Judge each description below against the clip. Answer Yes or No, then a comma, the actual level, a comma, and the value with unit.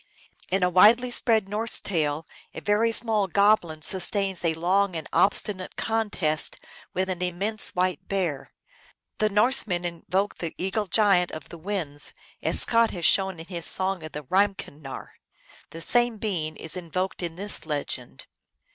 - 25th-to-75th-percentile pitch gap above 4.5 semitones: No, average, 3.9 semitones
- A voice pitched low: No, medium, 185 Hz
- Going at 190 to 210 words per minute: No, average, 155 wpm